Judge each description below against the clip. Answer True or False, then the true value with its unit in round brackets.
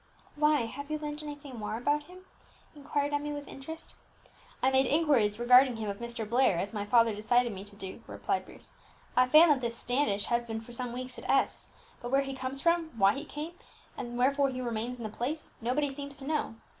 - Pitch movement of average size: True (3.9 semitones)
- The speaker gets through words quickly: True (215 wpm)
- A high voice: True (255 Hz)